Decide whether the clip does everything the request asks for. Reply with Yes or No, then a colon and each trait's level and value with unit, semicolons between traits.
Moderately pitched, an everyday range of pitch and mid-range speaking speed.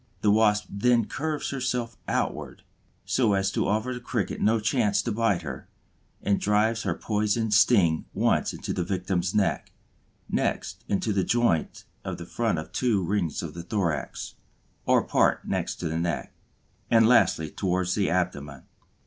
No: low, 105 Hz; average, 4.3 semitones; average, 155 wpm